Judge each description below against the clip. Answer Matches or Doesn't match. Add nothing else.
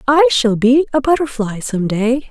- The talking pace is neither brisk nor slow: Matches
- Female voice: Matches